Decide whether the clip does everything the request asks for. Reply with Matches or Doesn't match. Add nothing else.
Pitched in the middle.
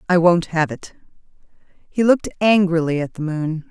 Matches